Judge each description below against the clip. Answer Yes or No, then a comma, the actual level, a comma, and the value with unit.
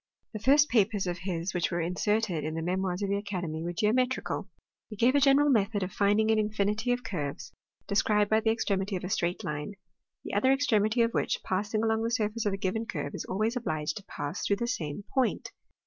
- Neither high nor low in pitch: No, high, 205 Hz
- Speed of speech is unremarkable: No, fast, 215 wpm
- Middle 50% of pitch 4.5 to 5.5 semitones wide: No, average, 3.7 semitones